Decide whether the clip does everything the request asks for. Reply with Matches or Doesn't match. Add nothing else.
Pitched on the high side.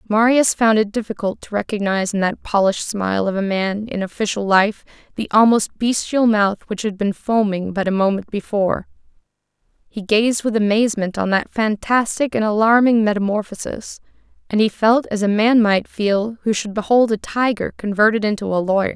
Matches